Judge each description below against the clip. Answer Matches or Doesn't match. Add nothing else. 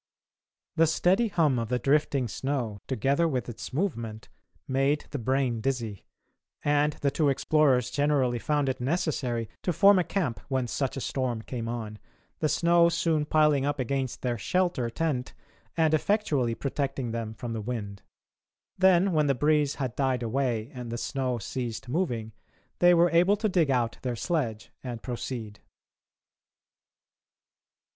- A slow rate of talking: Doesn't match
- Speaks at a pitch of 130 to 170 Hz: Matches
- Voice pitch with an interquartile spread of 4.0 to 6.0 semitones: Matches